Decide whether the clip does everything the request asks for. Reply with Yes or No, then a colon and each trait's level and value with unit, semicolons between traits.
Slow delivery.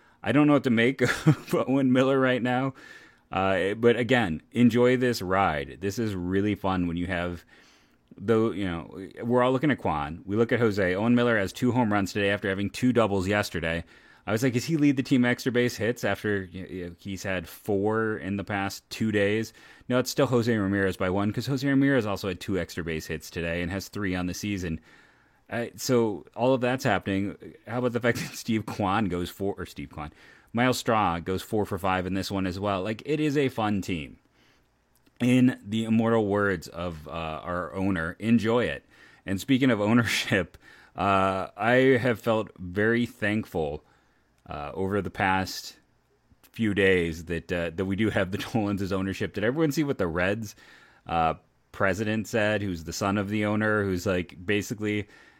No: average, 200 wpm